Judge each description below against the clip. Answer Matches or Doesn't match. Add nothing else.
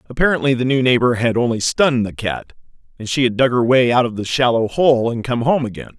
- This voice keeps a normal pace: Doesn't match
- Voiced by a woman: Doesn't match